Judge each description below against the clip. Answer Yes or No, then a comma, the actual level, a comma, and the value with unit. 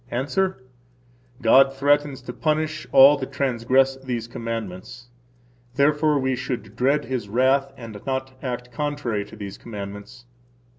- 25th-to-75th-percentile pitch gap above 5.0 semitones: No, average, 3.3 semitones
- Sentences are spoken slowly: Yes, slow, 130 wpm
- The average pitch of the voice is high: No, low, 130 Hz